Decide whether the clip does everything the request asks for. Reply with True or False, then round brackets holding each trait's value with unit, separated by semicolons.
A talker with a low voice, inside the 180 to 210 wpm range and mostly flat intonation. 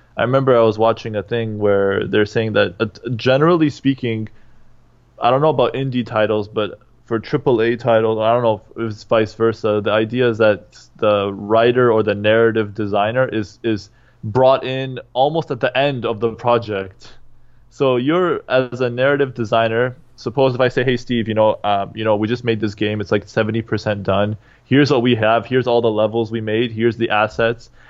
True (115 Hz; 200 wpm; 2.3 semitones)